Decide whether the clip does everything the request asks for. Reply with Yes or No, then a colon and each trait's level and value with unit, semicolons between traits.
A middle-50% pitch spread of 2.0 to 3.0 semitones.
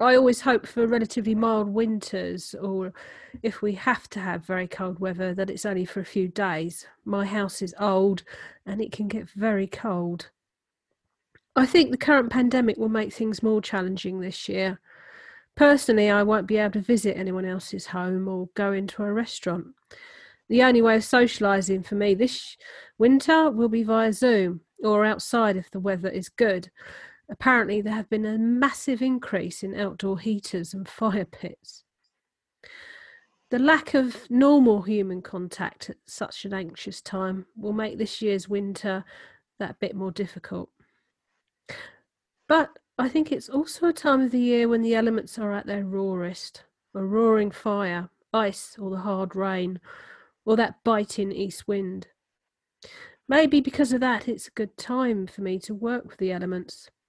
No: average, 3.8 semitones